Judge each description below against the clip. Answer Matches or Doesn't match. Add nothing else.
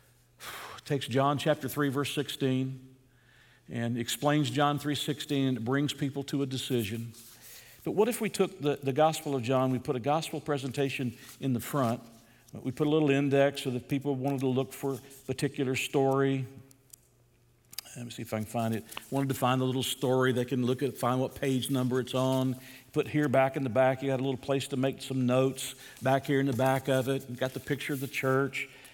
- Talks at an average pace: Doesn't match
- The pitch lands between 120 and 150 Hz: Matches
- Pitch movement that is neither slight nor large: Doesn't match